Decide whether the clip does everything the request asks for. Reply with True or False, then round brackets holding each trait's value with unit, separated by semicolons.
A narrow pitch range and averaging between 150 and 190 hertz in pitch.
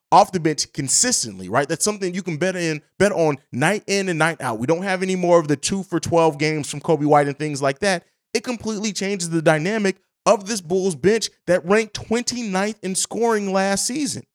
False (4.5 semitones; 185 Hz)